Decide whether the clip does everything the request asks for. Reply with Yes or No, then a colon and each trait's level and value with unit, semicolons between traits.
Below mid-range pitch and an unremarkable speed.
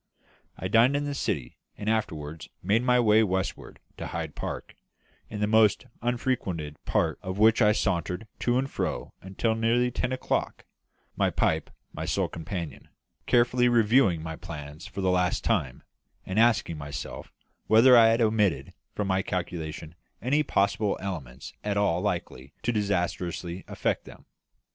Yes: low, 100 Hz; average, 155 wpm